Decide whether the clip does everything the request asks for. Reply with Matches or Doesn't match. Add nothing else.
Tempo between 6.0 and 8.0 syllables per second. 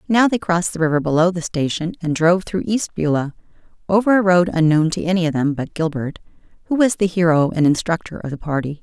Matches